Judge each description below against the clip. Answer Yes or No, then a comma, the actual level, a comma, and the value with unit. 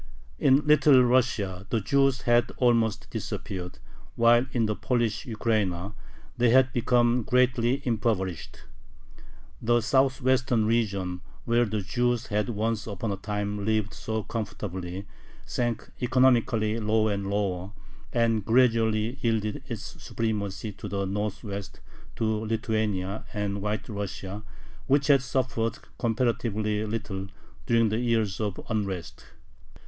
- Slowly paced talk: Yes, slow, 120 wpm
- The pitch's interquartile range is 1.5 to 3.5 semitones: Yes, average, 2.9 semitones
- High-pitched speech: No, low, 110 Hz